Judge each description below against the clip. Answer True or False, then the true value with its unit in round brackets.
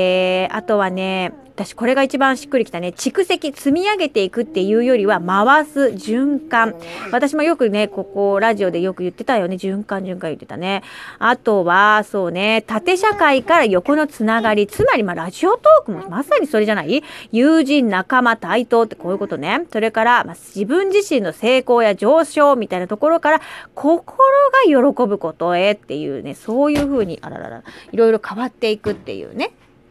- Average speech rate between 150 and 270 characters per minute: False (360 characters per minute)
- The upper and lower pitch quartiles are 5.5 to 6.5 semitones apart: True (6.2 semitones)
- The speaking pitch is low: False (230 Hz)